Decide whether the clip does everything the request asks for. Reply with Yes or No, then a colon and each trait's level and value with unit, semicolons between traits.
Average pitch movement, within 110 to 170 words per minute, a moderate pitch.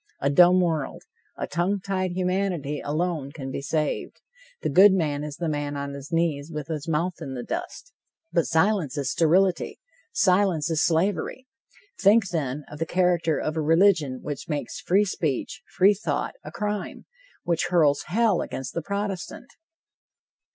Yes: average, 4.2 semitones; average, 160 wpm; medium, 165 Hz